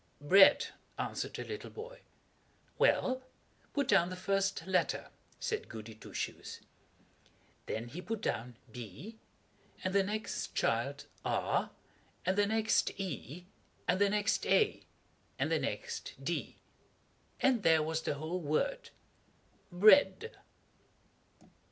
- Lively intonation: Yes, wide, 5.9 semitones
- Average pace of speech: No, slow, 120 wpm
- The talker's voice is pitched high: Yes, high, 195 Hz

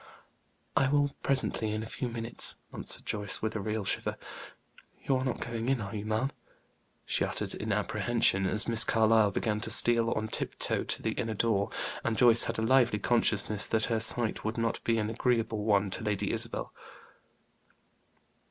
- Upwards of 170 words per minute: Yes, average, 180 wpm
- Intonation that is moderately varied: No, narrow, 1.7 semitones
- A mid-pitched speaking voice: No, low, 110 Hz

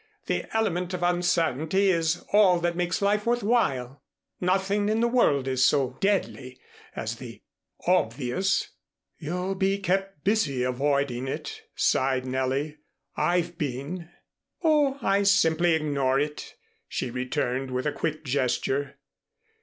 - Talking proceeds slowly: Yes, slow, 130 wpm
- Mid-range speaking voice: Yes, medium, 160 Hz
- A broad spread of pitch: Yes, wide, 6.2 semitones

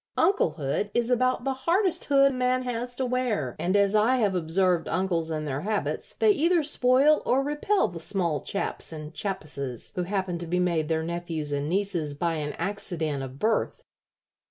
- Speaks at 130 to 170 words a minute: No, average, 180 wpm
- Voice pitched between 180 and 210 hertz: Yes, high, 190 Hz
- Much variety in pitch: Yes, wide, 7.9 semitones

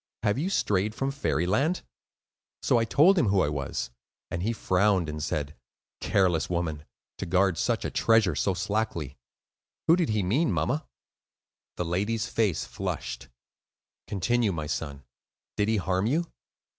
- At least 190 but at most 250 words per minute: No, average, 150 wpm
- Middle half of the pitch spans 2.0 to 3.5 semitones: No, average, 5.3 semitones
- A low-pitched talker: Yes, low, 100 Hz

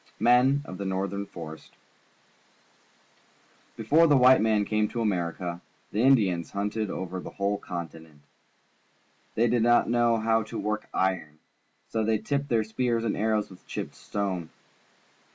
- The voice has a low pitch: Yes, low, 105 Hz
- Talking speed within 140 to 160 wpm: Yes, average, 155 wpm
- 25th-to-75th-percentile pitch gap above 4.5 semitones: No, average, 3.8 semitones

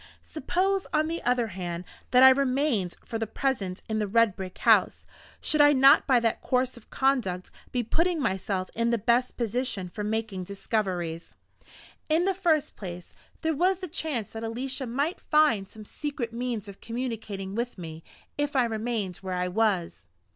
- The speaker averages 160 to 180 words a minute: Yes, average, 175 wpm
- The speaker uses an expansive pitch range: Yes, wide, 5.8 semitones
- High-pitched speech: Yes, high, 230 Hz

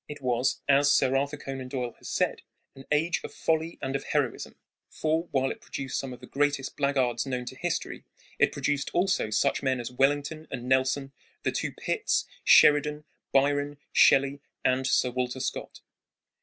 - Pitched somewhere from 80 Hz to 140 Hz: Yes, low, 135 Hz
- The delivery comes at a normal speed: Yes, average, 175 wpm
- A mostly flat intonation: Yes, narrow, 2.0 semitones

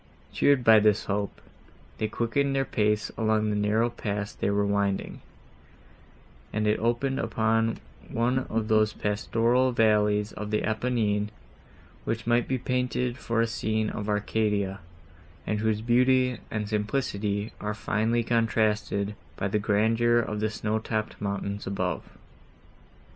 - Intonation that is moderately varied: No, narrow, 2.0 semitones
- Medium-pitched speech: No, low, 110 Hz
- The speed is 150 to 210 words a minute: No, slow, 135 wpm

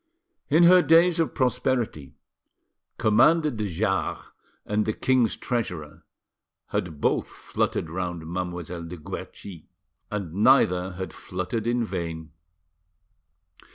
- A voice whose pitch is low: Yes, low, 100 Hz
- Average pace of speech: No, slow, 110 wpm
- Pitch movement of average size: No, wide, 6.5 semitones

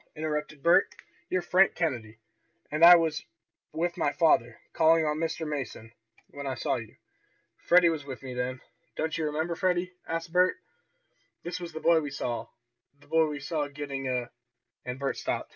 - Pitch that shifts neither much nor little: Yes, average, 3.5 semitones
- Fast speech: No, average, 175 wpm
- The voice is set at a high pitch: No, medium, 155 Hz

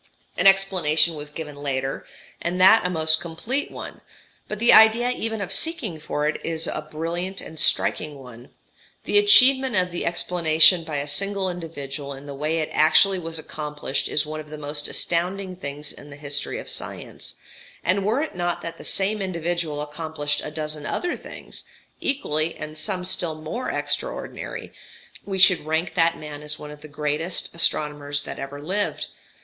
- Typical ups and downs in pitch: Yes, average, 4.0 semitones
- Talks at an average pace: Yes, average, 175 wpm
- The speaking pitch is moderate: Yes, medium, 160 Hz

